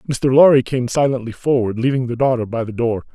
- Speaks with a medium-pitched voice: No, low, 125 Hz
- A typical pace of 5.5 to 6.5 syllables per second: Yes, 5.9 syllables/s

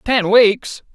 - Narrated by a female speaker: No, male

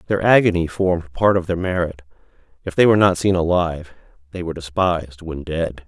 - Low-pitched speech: Yes, very low, 85 Hz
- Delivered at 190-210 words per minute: No, average, 175 wpm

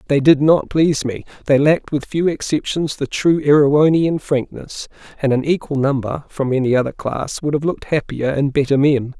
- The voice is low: No, medium, 145 Hz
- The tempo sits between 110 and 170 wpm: No, average, 190 wpm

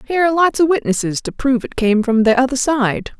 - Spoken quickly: Yes, fast, 245 wpm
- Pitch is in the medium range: No, very high, 255 Hz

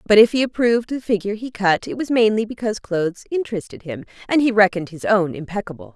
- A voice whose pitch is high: Yes, high, 205 Hz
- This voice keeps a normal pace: No, fast, 210 wpm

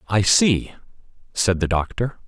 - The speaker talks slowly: Yes, slow, 130 wpm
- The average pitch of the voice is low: Yes, low, 105 Hz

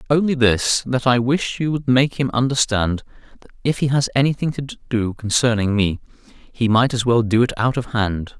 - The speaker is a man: Yes, male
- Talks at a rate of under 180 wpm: No, average, 200 wpm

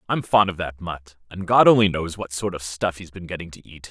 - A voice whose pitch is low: Yes, very low, 90 Hz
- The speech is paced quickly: Yes, fast, 275 wpm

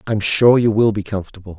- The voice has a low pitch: Yes, low, 105 Hz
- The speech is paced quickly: Yes, fast, 225 wpm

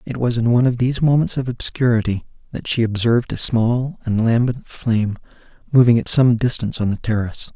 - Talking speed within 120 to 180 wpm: No, average, 190 wpm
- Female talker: No, male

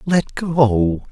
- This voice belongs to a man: Yes, male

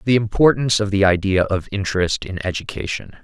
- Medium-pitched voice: No, low, 100 Hz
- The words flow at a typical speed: Yes, average, 165 wpm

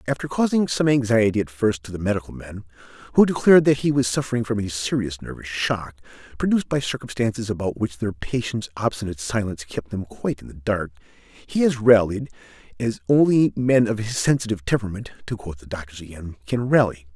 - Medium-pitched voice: No, low, 110 Hz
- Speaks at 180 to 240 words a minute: Yes, average, 185 wpm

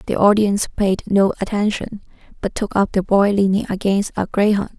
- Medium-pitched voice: No, high, 200 Hz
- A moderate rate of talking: Yes, average, 175 wpm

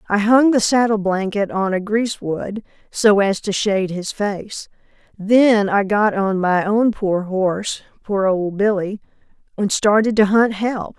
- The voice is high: Yes, high, 205 Hz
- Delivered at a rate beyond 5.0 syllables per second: No, 4.1 syllables/s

